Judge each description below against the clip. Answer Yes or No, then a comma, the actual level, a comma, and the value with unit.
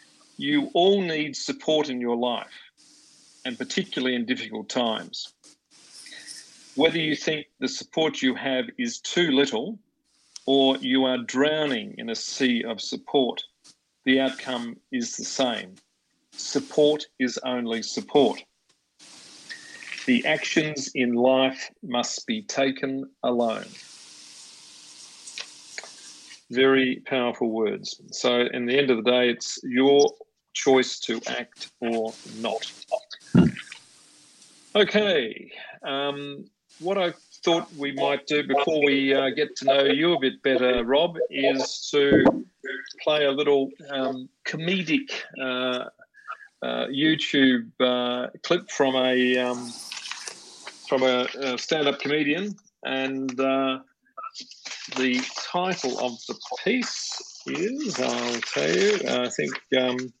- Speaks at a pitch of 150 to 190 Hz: No, low, 135 Hz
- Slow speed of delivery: Yes, slow, 115 wpm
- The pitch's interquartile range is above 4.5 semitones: Yes, average, 5.2 semitones